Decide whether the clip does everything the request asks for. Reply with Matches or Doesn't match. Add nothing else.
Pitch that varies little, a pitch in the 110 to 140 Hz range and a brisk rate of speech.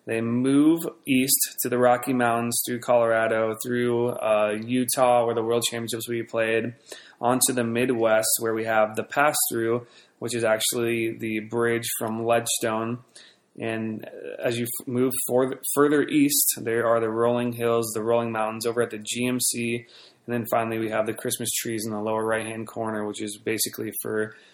Doesn't match